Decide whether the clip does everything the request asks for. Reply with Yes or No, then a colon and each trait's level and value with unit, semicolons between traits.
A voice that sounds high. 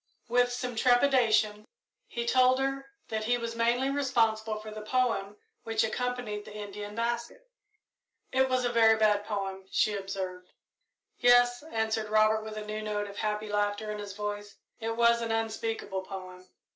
Yes: high, 220 Hz